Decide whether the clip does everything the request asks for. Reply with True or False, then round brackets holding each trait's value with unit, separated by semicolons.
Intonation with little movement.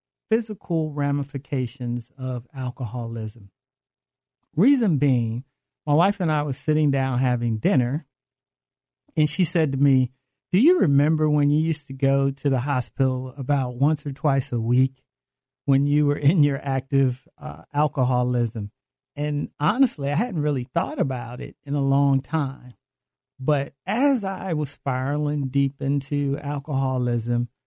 True (2.2 semitones)